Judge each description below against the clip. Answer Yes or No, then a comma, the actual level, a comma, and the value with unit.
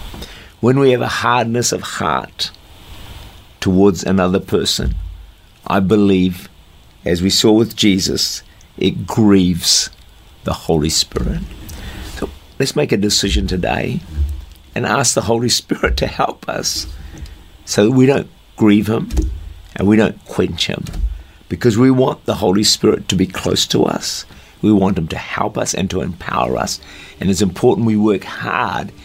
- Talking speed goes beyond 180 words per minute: No, average, 155 wpm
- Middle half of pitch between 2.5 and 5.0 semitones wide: No, wide, 5.4 semitones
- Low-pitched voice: Yes, very low, 95 Hz